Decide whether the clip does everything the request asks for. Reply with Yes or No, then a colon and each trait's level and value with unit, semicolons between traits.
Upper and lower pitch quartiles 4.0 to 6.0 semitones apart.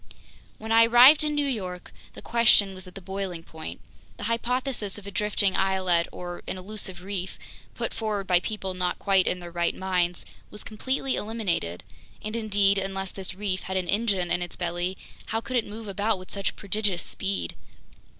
No: average, 3.1 semitones